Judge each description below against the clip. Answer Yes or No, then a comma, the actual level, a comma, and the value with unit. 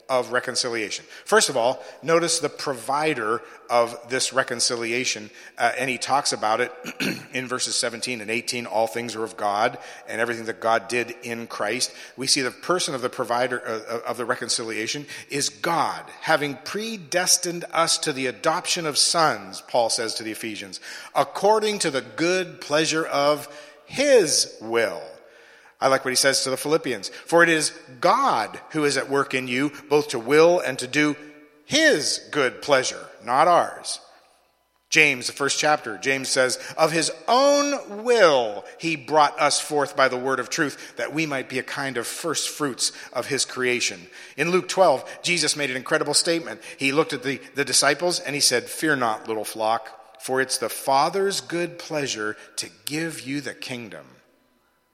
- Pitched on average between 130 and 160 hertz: Yes, medium, 140 Hz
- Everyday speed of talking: Yes, average, 175 wpm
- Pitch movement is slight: No, average, 4.8 semitones